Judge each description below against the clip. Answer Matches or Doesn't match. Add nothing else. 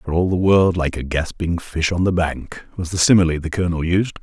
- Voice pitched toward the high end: Doesn't match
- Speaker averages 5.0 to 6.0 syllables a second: Matches